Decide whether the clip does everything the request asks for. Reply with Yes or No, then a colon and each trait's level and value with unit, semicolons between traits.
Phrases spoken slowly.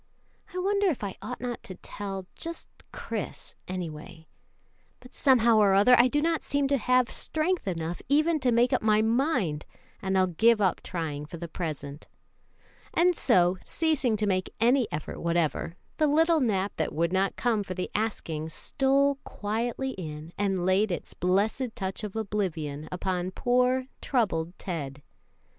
No: average, 160 wpm